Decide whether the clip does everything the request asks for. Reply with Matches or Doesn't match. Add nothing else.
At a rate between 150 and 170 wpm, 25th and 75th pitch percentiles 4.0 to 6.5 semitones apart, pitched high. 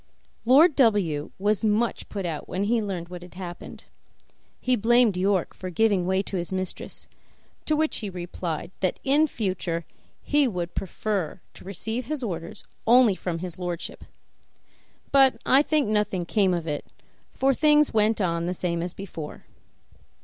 Matches